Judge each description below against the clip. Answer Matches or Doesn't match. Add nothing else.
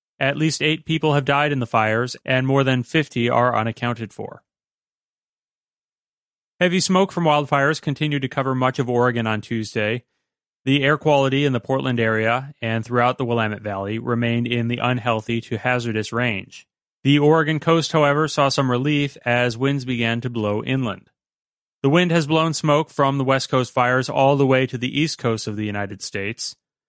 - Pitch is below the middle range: Matches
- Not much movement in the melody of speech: Doesn't match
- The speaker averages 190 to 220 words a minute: Doesn't match